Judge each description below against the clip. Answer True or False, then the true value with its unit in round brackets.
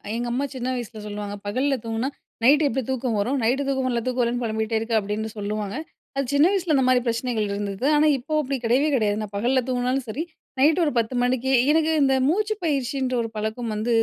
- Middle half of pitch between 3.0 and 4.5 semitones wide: True (3.6 semitones)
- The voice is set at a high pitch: True (245 Hz)